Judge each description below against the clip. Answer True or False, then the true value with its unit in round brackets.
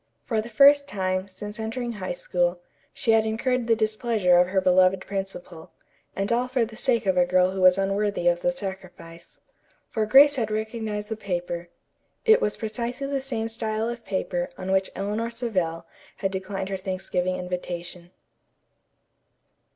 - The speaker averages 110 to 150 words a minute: False (165 wpm)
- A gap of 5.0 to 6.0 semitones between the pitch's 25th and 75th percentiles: False (4.0 semitones)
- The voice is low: False (210 Hz)